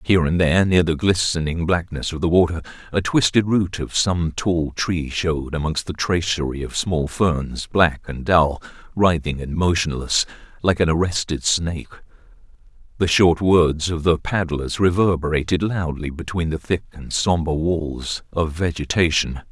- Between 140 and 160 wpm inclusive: Yes, average, 155 wpm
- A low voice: Yes, very low, 85 Hz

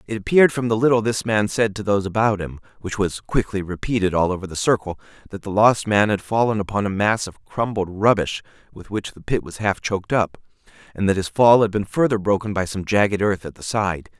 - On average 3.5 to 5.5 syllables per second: No, 5.8 syllables/s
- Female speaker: No, male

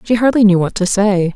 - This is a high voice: Yes, high, 205 Hz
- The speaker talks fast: Yes, fast, 265 wpm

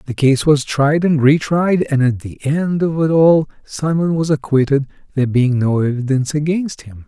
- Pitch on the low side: No, medium, 145 Hz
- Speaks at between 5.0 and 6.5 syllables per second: No, 4.8 syllables/s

